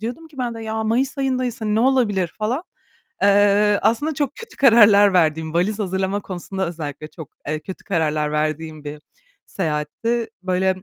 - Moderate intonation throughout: No, wide, 6.3 semitones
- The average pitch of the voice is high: Yes, high, 200 Hz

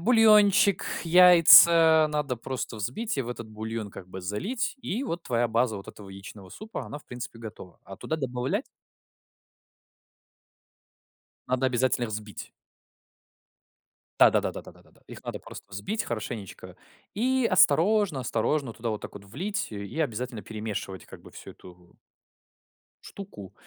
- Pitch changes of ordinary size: No, wide, 8.5 semitones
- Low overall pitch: Yes, low, 125 Hz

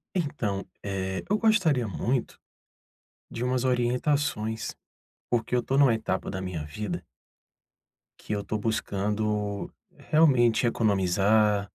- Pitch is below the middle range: Yes, low, 110 Hz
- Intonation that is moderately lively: Yes, average, 3.9 semitones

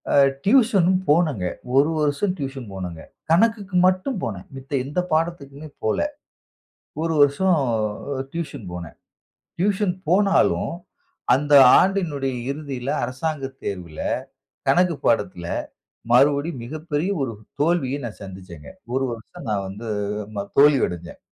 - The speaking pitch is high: No, medium, 145 Hz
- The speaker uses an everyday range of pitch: No, wide, 6.7 semitones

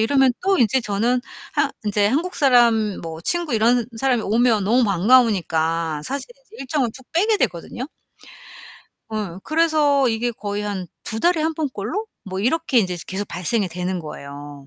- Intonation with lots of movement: Yes, wide, 5.9 semitones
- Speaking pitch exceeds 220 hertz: Yes, high, 230 Hz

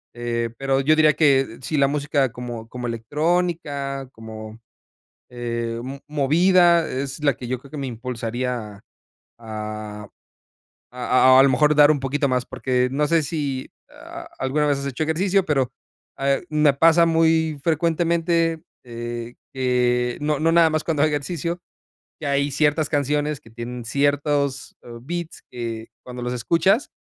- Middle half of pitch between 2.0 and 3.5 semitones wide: No, average, 4.1 semitones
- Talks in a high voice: No, medium, 140 Hz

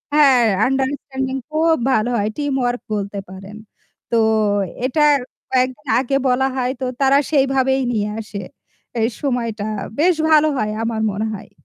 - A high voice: Yes, very high, 255 Hz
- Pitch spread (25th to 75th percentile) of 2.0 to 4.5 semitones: Yes, average, 3.6 semitones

